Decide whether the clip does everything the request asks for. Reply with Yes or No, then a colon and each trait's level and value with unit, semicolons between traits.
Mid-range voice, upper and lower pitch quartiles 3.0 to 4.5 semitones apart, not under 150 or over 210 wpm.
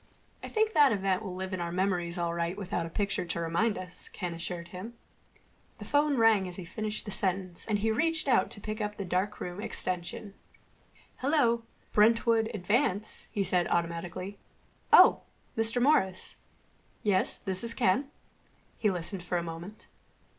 No: high, 195 Hz; average, 4.0 semitones; average, 165 wpm